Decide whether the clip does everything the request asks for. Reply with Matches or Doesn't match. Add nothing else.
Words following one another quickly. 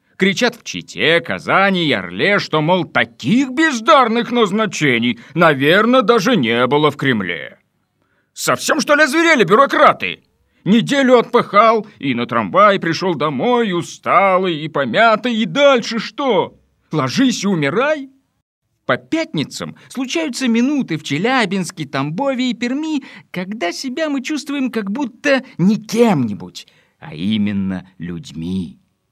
Doesn't match